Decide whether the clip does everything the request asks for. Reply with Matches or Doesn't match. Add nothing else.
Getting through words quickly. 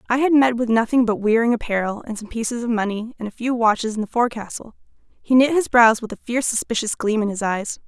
Matches